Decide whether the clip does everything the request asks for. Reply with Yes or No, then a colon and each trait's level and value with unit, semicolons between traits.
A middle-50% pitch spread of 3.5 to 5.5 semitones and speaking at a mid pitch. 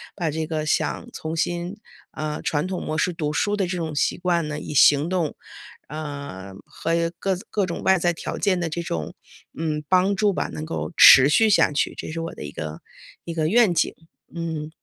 No: average, 2.9 semitones; medium, 165 Hz